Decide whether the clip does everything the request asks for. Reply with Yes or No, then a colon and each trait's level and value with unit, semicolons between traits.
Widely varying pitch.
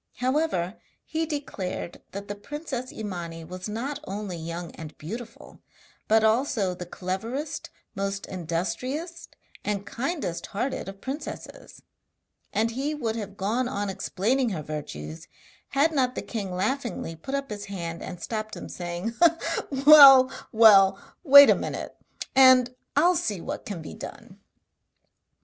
Yes: wide, 6.4 semitones